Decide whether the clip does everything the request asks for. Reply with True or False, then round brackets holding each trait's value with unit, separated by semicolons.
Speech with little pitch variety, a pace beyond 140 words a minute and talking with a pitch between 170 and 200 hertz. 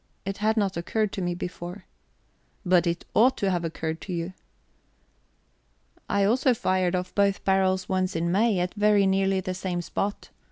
True (2.2 semitones; 170 wpm; 190 Hz)